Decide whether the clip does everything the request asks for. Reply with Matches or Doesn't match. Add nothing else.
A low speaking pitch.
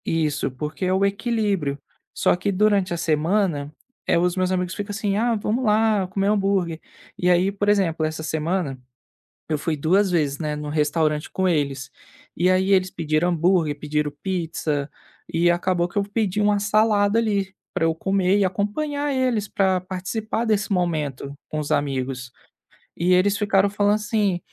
Doesn't match